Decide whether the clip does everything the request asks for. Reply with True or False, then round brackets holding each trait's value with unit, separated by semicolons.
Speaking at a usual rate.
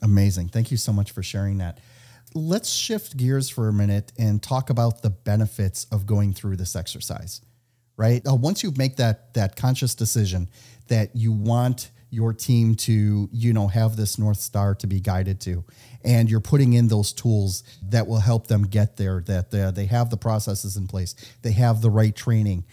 True (190 wpm)